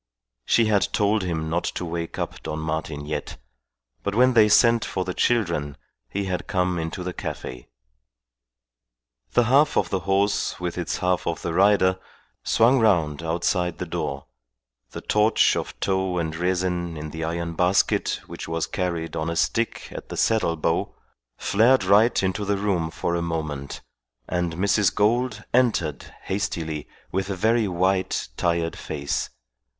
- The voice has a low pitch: Yes, very low, 90 Hz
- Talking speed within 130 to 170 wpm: Yes, average, 160 wpm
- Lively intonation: No, average, 3.8 semitones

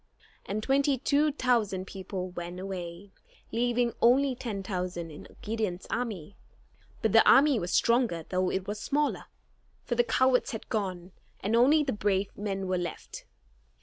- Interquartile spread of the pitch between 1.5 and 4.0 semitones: No, average, 5.0 semitones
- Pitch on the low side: No, high, 210 Hz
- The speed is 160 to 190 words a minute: No, average, 150 wpm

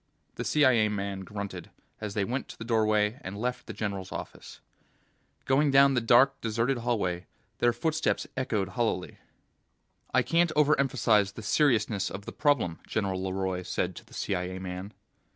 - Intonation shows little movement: No, average, 4.7 semitones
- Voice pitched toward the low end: Yes, low, 110 Hz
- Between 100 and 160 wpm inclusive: Yes, average, 155 wpm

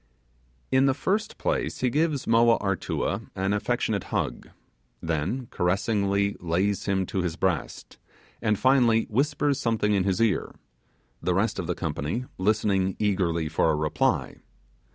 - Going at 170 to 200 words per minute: No, average, 140 wpm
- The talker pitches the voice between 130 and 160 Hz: No, low, 100 Hz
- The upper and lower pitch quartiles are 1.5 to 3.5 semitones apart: No, average, 4.2 semitones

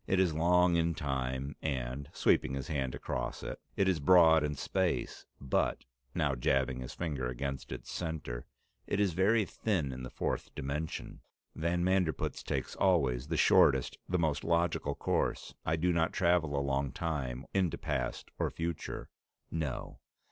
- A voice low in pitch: Yes, very low, 80 Hz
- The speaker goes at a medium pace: Yes, average, 155 wpm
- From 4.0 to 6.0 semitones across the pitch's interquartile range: Yes, average, 4.5 semitones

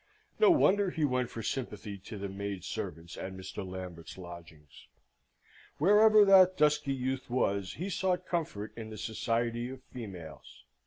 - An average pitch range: No, wide, 8.0 semitones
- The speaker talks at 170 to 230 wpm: No, average, 150 wpm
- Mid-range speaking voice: No, low, 115 Hz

